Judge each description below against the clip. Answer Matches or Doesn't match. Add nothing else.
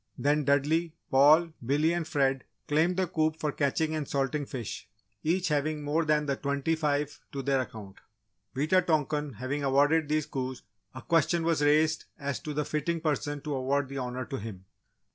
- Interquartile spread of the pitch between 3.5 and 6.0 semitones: Doesn't match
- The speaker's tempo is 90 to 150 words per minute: Doesn't match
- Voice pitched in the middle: Matches